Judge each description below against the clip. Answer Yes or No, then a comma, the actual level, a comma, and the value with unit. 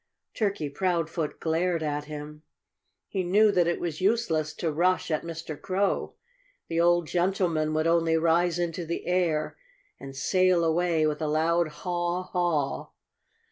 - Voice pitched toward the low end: No, medium, 170 Hz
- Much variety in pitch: No, narrow, 2.4 semitones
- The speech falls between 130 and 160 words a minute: Yes, average, 145 wpm